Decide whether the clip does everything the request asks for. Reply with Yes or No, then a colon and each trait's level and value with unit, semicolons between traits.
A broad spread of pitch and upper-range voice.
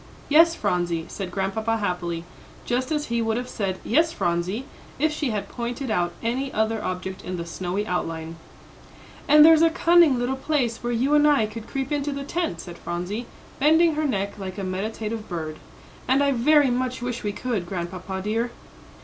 Yes: wide, 6.7 semitones; high, 225 Hz